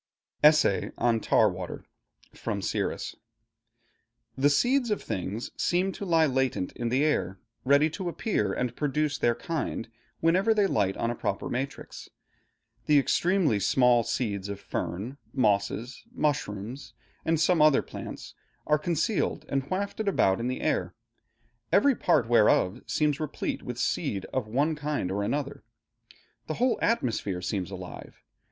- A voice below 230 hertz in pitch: Yes, low, 135 Hz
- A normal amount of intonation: No, wide, 6.9 semitones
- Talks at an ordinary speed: Yes, average, 145 wpm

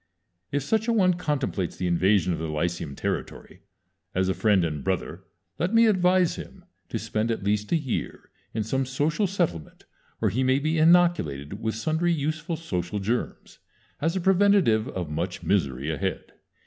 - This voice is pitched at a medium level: No, low, 115 Hz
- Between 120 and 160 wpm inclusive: No, average, 170 wpm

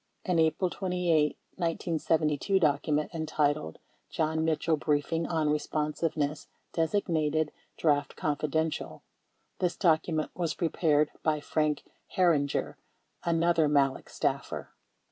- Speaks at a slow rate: Yes, slow, 95 wpm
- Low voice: No, medium, 155 Hz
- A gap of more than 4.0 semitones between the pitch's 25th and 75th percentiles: No, narrow, 1.8 semitones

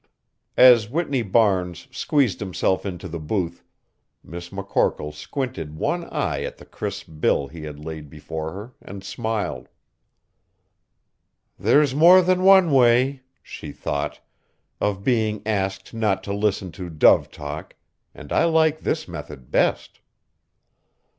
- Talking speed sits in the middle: No, slow, 130 wpm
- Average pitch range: No, wide, 7.3 semitones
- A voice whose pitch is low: Yes, low, 100 Hz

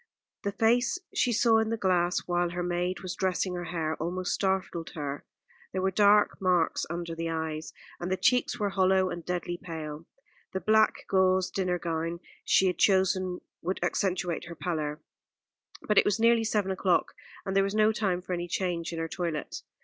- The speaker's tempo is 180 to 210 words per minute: Yes, average, 185 wpm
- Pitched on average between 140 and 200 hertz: Yes, medium, 185 Hz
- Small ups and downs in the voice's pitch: Yes, narrow, 2.3 semitones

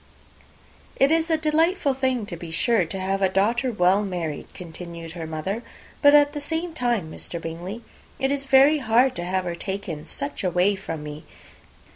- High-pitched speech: Yes, high, 200 Hz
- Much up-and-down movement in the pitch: Yes, wide, 7.7 semitones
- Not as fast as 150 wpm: No, average, 175 wpm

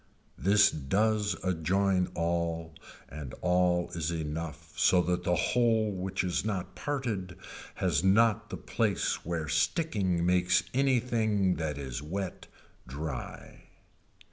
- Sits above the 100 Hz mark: No, very low, 90 Hz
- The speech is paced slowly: Yes, slow, 115 wpm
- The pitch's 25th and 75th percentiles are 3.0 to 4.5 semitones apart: Yes, average, 3.9 semitones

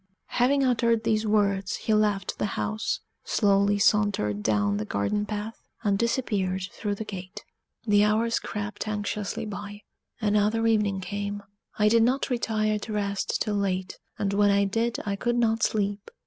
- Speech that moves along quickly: No, average, 160 wpm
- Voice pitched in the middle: No, high, 210 Hz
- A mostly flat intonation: Yes, narrow, 1.7 semitones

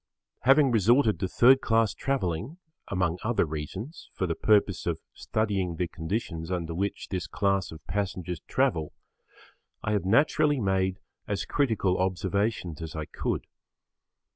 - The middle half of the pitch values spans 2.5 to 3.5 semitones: No, average, 4.2 semitones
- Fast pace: No, average, 140 wpm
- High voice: No, very low, 95 Hz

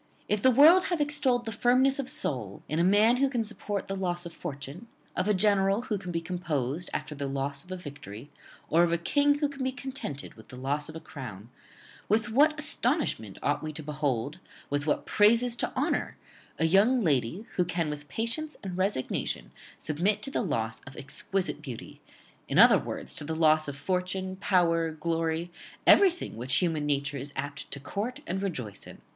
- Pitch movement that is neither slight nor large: No, wide, 7.4 semitones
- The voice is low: No, medium, 175 Hz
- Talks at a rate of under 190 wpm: No, average, 195 wpm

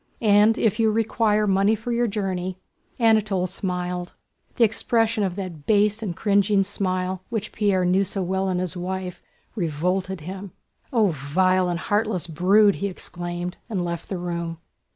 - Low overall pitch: No, high, 190 Hz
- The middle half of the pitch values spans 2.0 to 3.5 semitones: Yes, average, 2.8 semitones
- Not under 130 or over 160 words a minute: Yes, average, 155 wpm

